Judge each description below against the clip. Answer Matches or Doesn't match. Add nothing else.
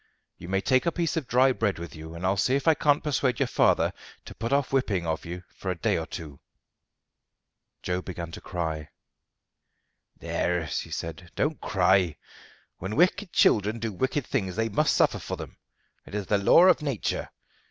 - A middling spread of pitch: Doesn't match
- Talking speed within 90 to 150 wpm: Doesn't match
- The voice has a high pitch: Doesn't match